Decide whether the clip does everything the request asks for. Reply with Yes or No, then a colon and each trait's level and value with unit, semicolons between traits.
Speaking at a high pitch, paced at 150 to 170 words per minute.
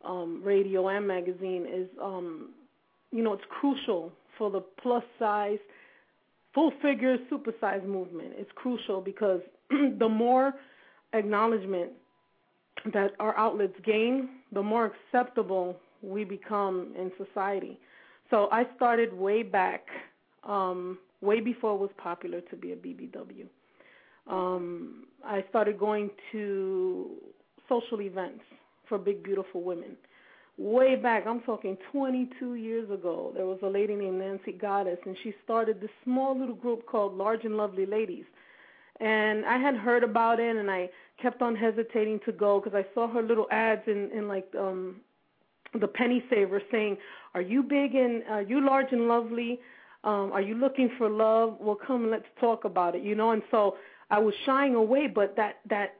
Yes: high, 215 Hz; average, 160 wpm